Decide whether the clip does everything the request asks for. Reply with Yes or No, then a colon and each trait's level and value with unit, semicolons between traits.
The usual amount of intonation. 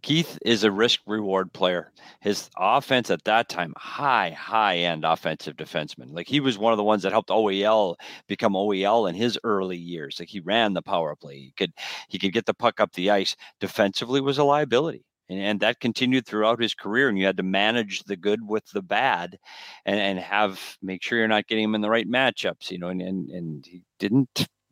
Yes: average, 3.5 semitones